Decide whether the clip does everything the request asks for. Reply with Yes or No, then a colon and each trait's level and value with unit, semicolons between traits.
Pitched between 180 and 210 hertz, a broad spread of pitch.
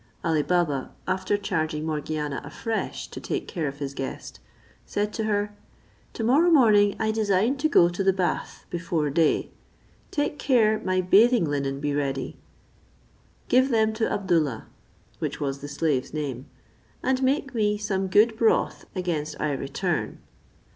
Yes: medium, 185 Hz; wide, 6.5 semitones